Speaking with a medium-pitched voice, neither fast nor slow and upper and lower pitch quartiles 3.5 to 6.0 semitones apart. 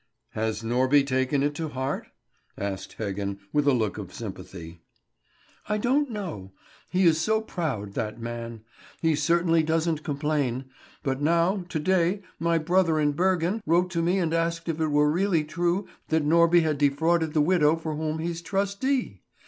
Yes: medium, 160 Hz; average, 165 wpm; average, 4.3 semitones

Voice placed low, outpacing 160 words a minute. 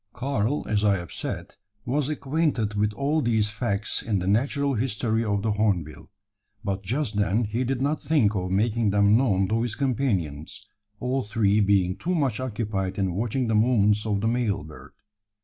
Yes: low, 110 Hz; average, 180 wpm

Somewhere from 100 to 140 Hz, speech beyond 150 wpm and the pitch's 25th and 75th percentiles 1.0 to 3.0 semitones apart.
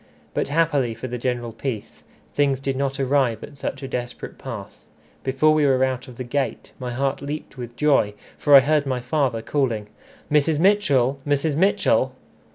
Yes: low, 135 Hz; average, 175 wpm; average, 2.7 semitones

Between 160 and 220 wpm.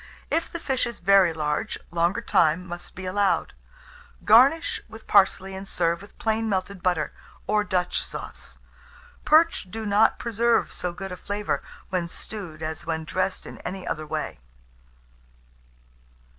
No: average, 145 wpm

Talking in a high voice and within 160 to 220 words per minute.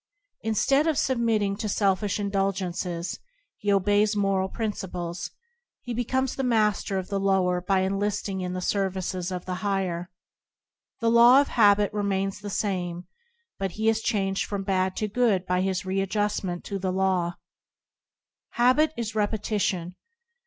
No: high, 195 Hz; average, 150 wpm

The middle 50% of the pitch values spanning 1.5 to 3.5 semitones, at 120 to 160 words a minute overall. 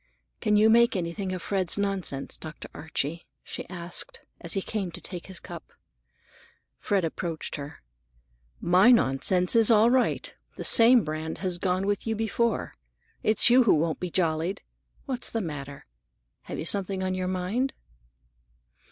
No: average, 4.3 semitones; average, 155 wpm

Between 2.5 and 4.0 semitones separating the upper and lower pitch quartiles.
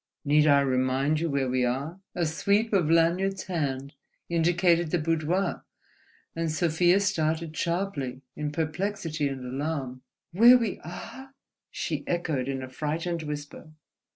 Yes: average, 3.7 semitones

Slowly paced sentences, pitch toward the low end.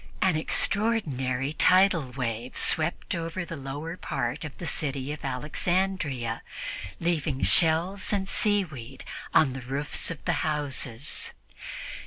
No: slow, 120 wpm; medium, 150 Hz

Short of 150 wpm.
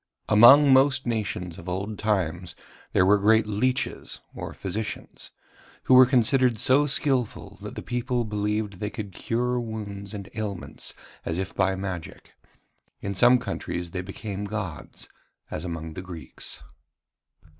Yes: average, 140 wpm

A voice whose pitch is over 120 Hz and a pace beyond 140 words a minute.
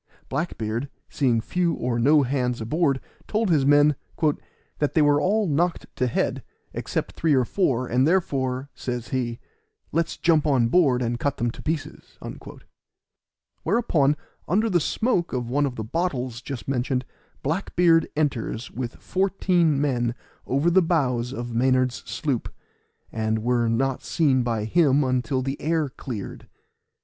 Yes: low, 135 Hz; average, 150 wpm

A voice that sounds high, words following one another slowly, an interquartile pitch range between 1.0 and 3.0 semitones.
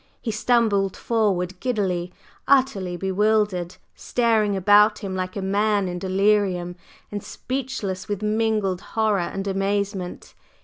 Yes: high, 200 Hz; slow, 120 wpm; narrow, 2.4 semitones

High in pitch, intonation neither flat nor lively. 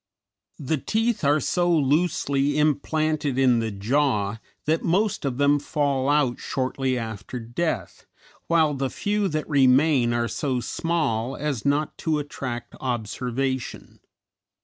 No: medium, 140 Hz; average, 3.6 semitones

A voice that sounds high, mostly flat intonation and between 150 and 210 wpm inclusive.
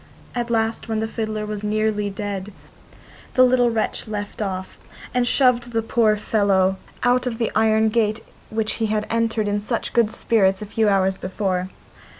Yes: high, 215 Hz; narrow, 1.9 semitones; average, 170 wpm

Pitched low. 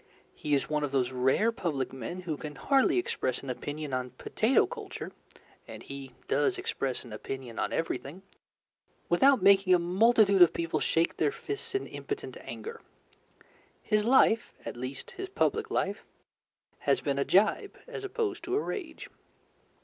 No: medium, 175 Hz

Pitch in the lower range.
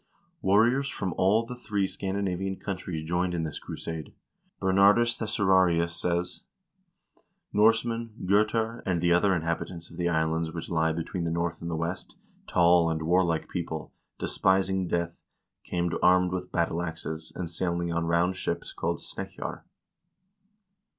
Yes: very low, 90 Hz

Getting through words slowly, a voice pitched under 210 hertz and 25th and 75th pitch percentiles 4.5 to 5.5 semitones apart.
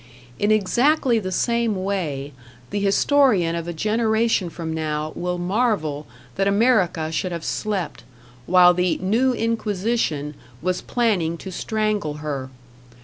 Yes: slow, 130 wpm; medium, 185 Hz; average, 5.0 semitones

